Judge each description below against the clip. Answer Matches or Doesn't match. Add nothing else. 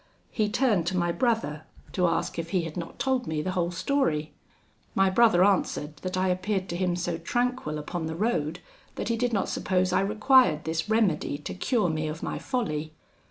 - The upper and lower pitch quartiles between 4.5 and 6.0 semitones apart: Matches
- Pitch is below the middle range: Doesn't match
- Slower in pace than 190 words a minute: Doesn't match